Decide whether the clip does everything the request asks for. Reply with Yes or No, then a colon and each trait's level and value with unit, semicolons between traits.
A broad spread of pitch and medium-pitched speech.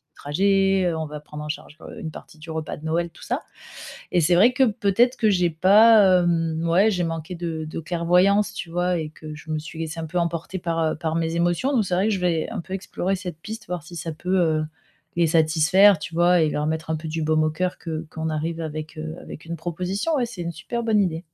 No: average, 2.9 semitones; medium, 170 Hz